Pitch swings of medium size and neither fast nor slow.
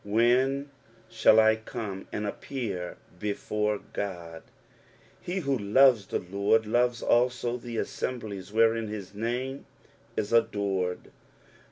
No: average, 3.3 semitones; slow, 120 wpm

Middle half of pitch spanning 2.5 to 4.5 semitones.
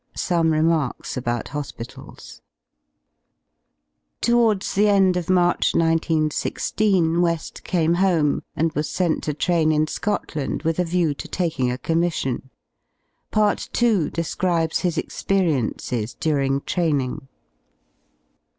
Yes: average, 3.3 semitones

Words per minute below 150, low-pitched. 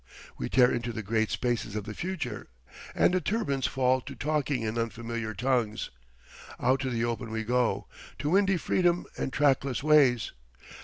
No: average, 165 wpm; low, 125 Hz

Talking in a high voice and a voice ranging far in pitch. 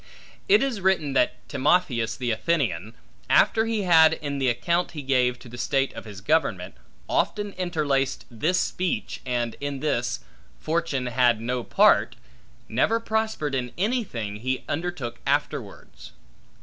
No: medium, 140 Hz; wide, 6.2 semitones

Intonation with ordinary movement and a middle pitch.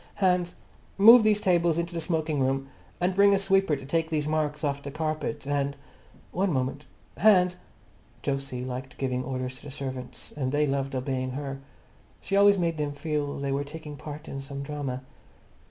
Yes: average, 3.7 semitones; medium, 145 Hz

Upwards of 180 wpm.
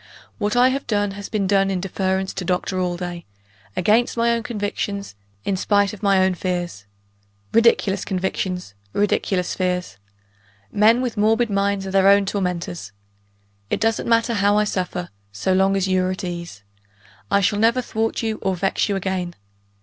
No: average, 170 wpm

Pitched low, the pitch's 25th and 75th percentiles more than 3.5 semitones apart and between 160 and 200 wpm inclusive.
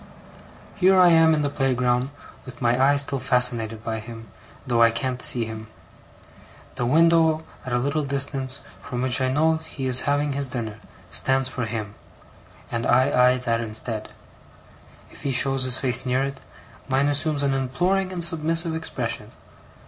No: low, 130 Hz; average, 3.0 semitones; average, 165 wpm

